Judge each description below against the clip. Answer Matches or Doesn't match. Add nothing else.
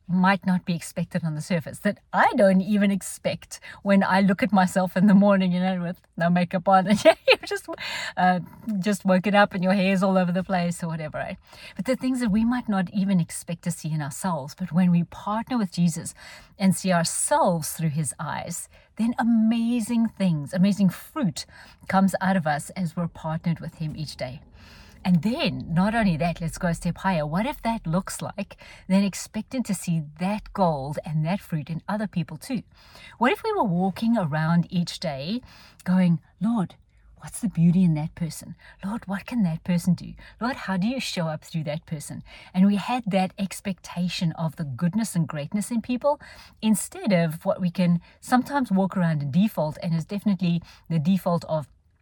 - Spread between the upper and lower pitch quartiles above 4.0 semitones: Doesn't match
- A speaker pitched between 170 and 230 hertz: Matches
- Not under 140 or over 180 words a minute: Doesn't match